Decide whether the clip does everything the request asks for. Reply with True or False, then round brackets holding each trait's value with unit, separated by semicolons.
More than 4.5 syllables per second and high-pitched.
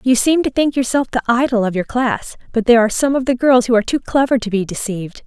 True (6.5 syllables/s; 240 Hz)